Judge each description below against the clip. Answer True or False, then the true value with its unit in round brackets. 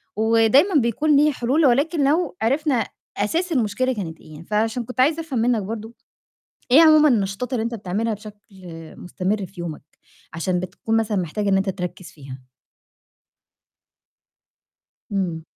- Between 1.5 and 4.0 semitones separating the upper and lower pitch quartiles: False (5.5 semitones)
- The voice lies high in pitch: True (225 Hz)